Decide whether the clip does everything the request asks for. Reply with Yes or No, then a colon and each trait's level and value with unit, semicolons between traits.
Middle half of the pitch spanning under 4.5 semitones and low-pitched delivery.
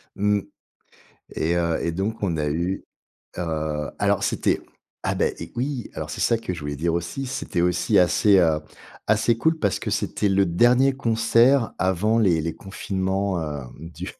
No: average, 5.2 semitones; very low, 95 Hz